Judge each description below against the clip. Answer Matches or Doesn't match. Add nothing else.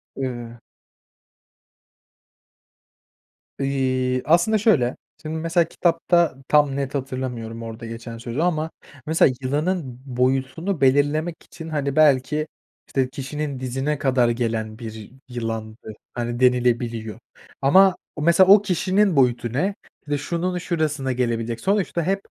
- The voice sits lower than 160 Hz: Matches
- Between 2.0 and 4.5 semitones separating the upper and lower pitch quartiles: Doesn't match